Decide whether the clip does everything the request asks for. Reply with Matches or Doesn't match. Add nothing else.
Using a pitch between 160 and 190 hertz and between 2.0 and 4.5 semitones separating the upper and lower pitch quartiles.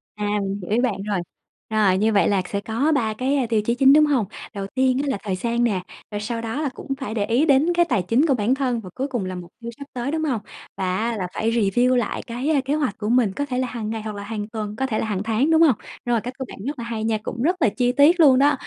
Doesn't match